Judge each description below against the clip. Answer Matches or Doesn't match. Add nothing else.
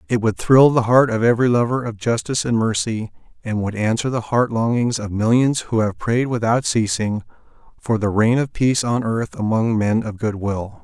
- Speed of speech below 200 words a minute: Doesn't match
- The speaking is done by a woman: Doesn't match